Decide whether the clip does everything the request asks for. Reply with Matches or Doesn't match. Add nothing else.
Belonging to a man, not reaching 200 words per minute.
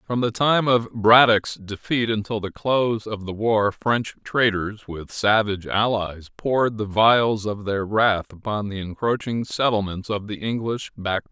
Matches